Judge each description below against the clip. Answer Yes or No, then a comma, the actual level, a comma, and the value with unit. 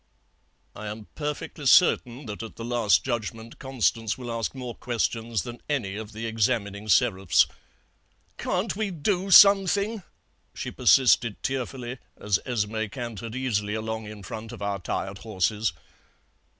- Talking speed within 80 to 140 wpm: Yes, slow, 135 wpm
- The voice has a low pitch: Yes, low, 115 Hz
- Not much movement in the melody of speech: No, average, 3.8 semitones